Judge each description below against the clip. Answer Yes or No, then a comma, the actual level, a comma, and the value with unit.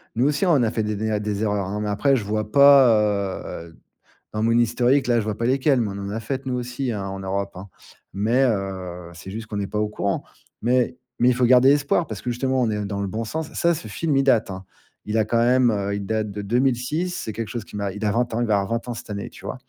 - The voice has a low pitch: Yes, low, 110 Hz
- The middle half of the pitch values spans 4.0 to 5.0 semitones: No, average, 3.6 semitones